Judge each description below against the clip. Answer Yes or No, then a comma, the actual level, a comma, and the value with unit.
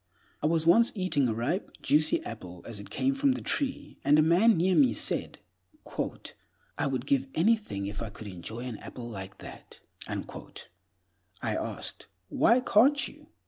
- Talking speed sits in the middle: Yes, average, 165 wpm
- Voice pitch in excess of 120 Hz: Yes, medium, 140 Hz